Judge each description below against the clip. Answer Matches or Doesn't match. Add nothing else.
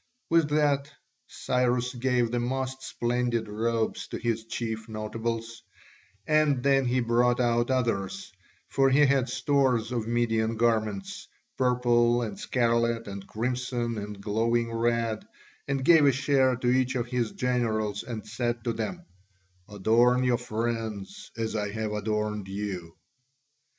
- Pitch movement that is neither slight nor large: Doesn't match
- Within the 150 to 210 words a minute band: Doesn't match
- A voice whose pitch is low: Matches